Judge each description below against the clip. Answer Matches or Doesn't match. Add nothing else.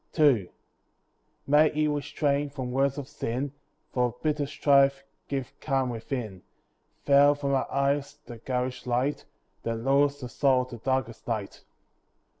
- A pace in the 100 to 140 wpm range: Matches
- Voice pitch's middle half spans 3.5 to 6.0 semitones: Doesn't match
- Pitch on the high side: Doesn't match